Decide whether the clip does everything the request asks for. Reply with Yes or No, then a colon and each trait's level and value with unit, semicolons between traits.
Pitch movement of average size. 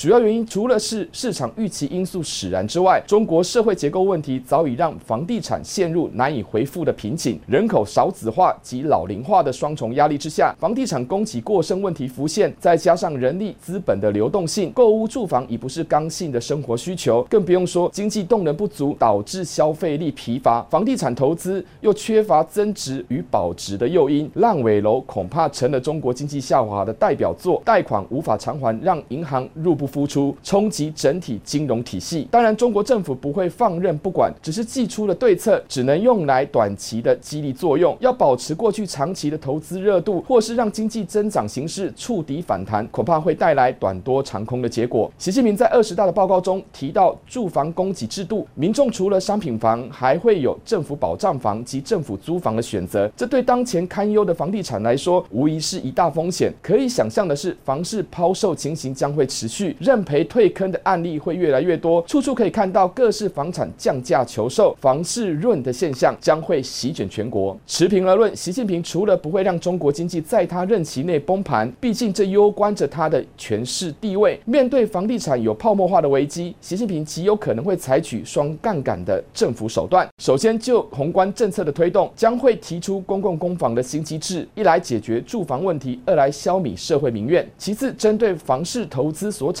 No: wide, 6.9 semitones